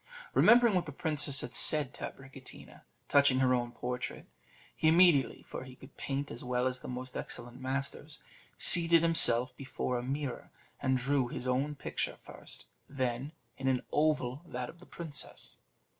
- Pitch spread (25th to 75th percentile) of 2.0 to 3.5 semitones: Yes, average, 2.9 semitones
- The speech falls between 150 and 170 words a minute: Yes, average, 165 wpm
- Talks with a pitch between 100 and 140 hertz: Yes, low, 135 Hz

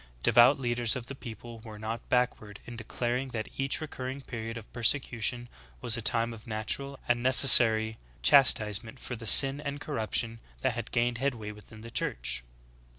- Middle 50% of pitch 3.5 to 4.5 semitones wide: No, narrow, 2.5 semitones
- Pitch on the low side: Yes, low, 120 Hz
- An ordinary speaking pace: Yes, average, 170 wpm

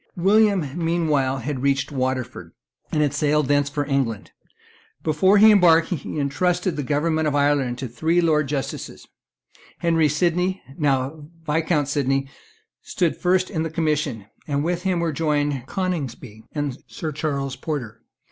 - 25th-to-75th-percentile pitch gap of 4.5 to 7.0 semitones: No, average, 3.4 semitones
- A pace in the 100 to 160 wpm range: Yes, average, 145 wpm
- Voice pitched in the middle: Yes, medium, 150 Hz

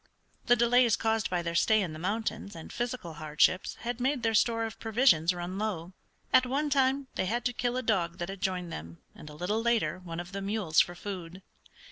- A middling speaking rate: No, fast, 215 wpm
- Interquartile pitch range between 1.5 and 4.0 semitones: No, wide, 5.4 semitones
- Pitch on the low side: No, high, 205 Hz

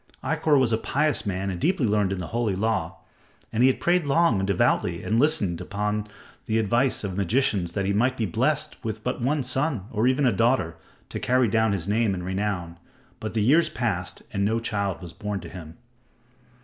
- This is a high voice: No, low, 110 Hz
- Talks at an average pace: No, fast, 210 wpm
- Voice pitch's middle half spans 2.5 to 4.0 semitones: No, average, 4.8 semitones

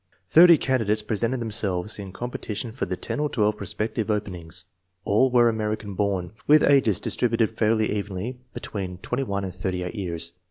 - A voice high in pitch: No, low, 105 Hz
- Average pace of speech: Yes, average, 160 wpm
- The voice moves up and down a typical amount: Yes, average, 3.5 semitones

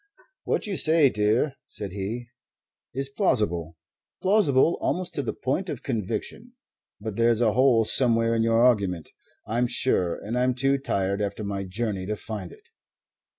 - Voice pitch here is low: Yes, low, 115 Hz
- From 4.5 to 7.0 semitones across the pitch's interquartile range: Yes, average, 4.8 semitones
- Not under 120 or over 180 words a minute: Yes, average, 155 wpm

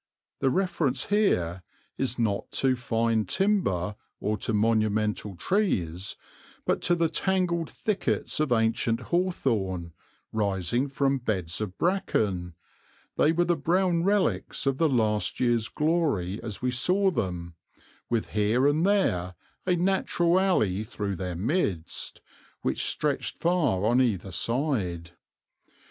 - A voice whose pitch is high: No, low, 120 Hz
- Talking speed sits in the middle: No, slow, 125 wpm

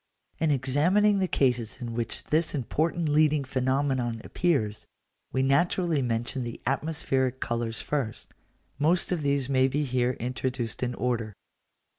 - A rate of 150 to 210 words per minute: No, slow, 135 wpm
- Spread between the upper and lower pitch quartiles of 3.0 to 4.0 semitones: Yes, average, 3.7 semitones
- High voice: No, low, 135 Hz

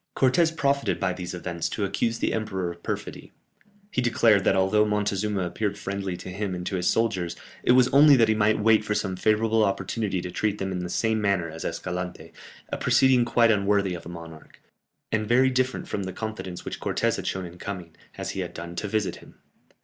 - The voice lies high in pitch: No, low, 100 Hz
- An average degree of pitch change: Yes, average, 3.6 semitones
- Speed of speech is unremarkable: No, fast, 210 wpm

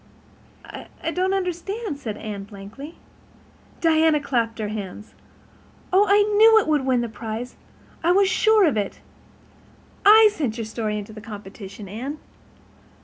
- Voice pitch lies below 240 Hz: No, very high, 260 Hz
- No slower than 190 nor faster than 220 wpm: No, average, 140 wpm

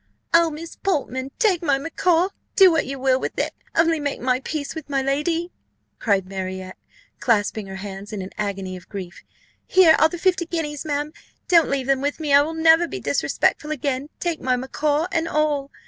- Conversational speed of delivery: Yes, average, 195 wpm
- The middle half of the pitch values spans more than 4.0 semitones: Yes, average, 4.4 semitones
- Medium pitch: No, very high, 290 Hz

